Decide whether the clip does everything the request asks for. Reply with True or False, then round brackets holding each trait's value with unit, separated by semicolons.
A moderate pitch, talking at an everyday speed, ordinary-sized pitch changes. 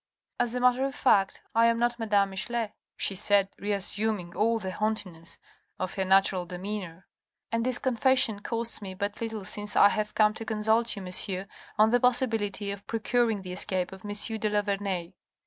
False (210 Hz; 185 wpm; 3.0 semitones)